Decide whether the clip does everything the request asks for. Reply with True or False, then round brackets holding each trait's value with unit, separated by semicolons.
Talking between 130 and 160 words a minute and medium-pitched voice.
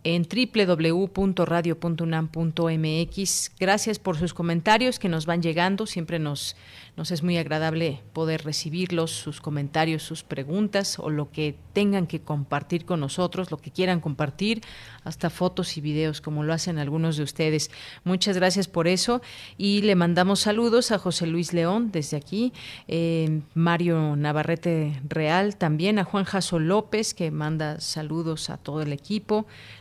True (150 wpm; 170 Hz)